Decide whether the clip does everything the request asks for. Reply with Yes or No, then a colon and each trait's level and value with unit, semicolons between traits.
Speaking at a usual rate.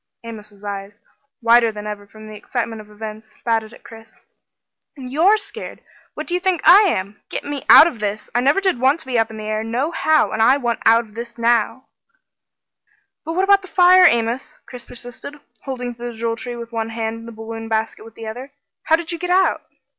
No: fast, 210 wpm